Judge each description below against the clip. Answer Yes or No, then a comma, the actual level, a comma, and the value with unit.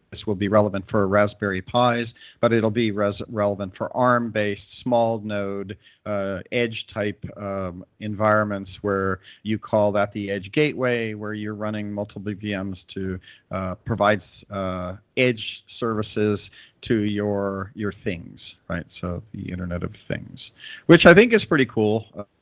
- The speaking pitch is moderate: No, low, 105 Hz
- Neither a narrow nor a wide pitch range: No, narrow, 2.1 semitones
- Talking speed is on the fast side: No, average, 145 wpm